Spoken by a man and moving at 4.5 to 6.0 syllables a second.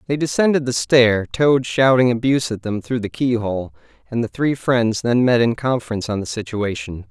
Yes: male; 5.3 syllables/s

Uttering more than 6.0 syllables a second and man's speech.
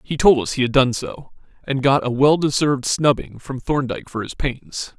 No: 5.0 syllables/s; male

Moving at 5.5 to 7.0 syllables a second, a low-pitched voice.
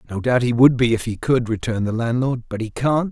Yes: 5.8 syllables/s; low, 120 Hz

